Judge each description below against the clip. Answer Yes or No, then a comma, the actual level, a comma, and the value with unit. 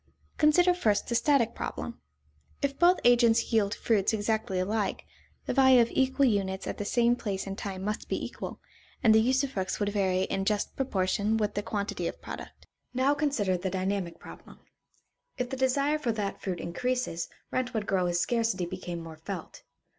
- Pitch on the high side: Yes, high, 215 Hz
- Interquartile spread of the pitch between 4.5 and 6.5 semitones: Yes, average, 4.8 semitones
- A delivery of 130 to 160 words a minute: No, average, 175 wpm